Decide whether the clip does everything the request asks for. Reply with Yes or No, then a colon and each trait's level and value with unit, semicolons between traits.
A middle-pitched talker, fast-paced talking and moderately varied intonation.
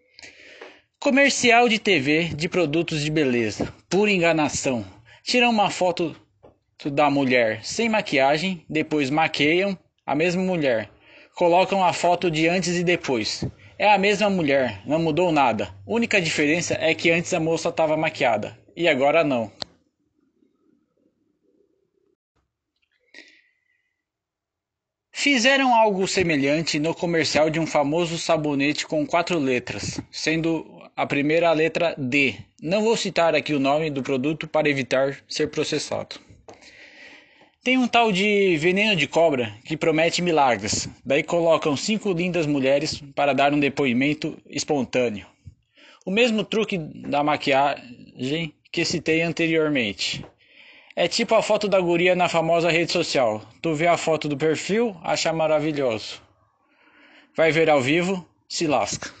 No: medium, 165 Hz; average, 130 wpm; average, 4.4 semitones